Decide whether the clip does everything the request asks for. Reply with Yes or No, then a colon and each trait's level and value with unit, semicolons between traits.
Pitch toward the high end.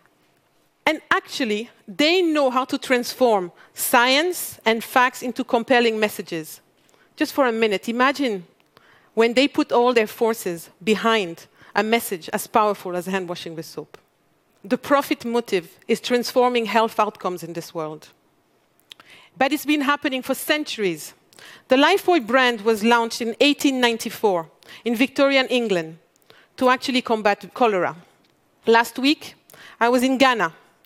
Yes: high, 235 Hz